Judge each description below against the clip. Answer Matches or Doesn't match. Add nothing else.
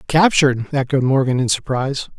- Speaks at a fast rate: Doesn't match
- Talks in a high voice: Doesn't match